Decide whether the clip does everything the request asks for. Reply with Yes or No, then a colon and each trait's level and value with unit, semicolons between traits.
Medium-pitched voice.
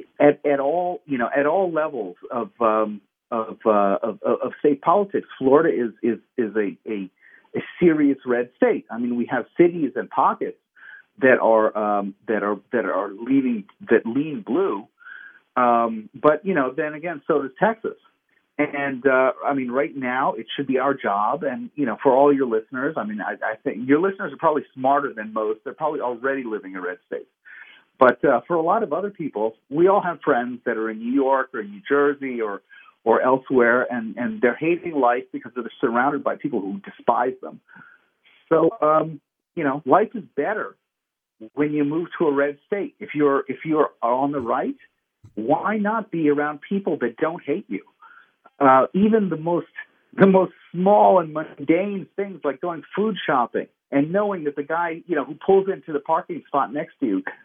Yes: medium, 145 Hz